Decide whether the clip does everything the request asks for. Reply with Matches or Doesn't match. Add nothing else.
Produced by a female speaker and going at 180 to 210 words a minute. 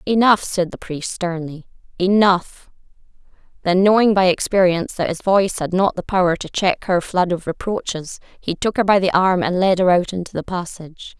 Matches